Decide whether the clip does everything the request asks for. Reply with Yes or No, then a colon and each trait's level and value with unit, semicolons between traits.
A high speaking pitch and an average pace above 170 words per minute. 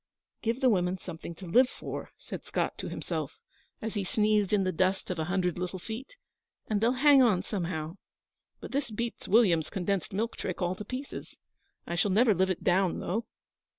Yes: high, 195 Hz; average, 190 wpm